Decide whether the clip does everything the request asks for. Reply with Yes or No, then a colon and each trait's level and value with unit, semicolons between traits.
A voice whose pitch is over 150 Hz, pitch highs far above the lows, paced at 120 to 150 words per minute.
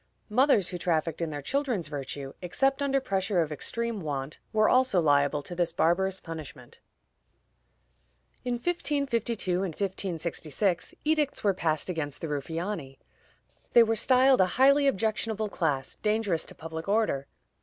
Yes: medium, 185 Hz; wide, 6.5 semitones; average, 145 wpm